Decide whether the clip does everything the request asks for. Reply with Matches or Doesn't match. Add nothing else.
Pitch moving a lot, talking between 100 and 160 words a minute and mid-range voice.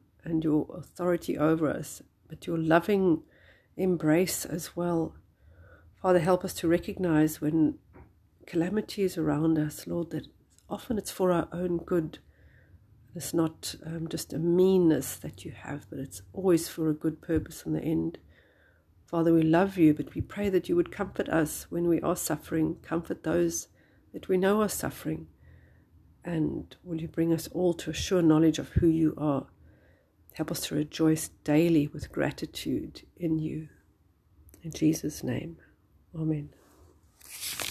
Matches